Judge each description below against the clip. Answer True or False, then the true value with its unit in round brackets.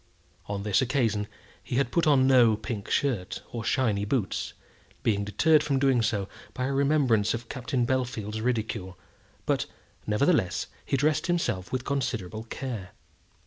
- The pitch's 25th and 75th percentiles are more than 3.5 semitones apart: True (4.4 semitones)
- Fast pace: False (145 wpm)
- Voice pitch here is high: False (120 Hz)